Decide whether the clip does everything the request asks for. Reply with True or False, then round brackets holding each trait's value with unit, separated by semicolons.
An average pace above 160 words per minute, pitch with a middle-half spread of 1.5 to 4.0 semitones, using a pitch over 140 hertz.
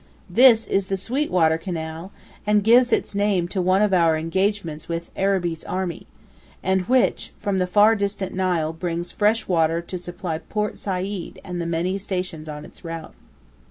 True (170 wpm; 3.3 semitones; 185 Hz)